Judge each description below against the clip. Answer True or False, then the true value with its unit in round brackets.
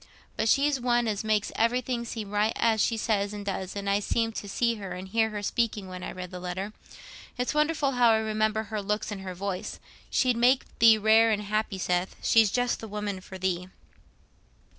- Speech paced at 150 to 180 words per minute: False (205 wpm)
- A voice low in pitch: False (215 Hz)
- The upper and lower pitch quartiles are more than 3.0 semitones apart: False (2.7 semitones)